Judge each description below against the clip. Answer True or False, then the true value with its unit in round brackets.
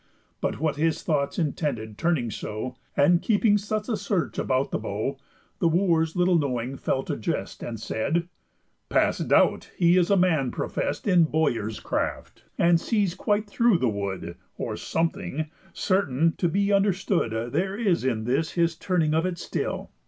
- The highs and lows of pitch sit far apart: True (6.1 semitones)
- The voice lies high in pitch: False (165 Hz)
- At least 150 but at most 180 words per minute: True (165 wpm)